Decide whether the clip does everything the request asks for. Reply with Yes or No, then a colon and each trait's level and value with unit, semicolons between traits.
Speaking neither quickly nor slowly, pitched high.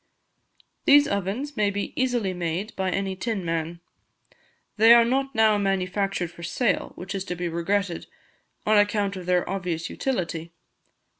Yes: average, 150 wpm; high, 195 Hz